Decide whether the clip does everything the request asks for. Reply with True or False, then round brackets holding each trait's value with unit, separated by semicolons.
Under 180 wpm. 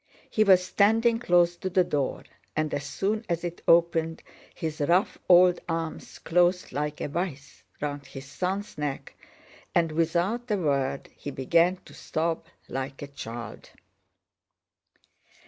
True (140 wpm)